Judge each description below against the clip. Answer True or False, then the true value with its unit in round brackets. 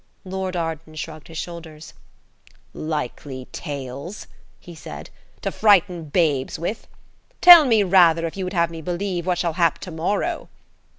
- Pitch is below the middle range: False (170 Hz)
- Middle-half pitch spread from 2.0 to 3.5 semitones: True (2.9 semitones)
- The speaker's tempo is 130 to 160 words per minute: True (145 wpm)